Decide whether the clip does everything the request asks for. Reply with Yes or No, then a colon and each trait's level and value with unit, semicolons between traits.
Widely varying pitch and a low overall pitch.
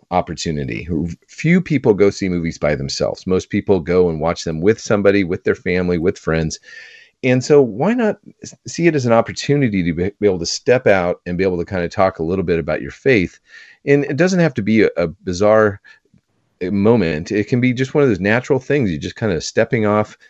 Yes: wide, 7.4 semitones; low, 105 Hz